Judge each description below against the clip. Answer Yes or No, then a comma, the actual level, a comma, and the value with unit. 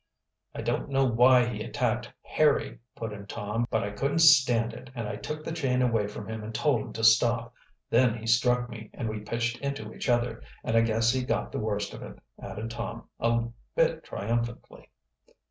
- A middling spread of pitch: No, narrow, 2.0 semitones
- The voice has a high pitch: No, low, 115 Hz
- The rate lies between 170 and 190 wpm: No, average, 200 wpm